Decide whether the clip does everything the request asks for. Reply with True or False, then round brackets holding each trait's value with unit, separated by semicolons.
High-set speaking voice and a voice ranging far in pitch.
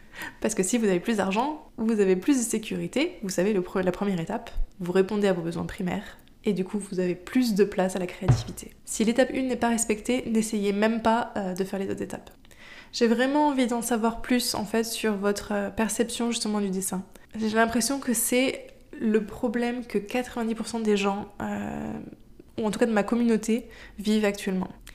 False (215 Hz; 3.4 semitones)